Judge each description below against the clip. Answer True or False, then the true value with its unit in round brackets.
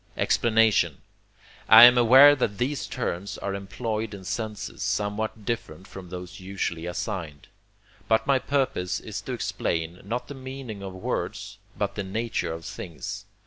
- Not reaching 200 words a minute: True (145 wpm)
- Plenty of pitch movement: False (4.3 semitones)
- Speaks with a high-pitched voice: False (105 Hz)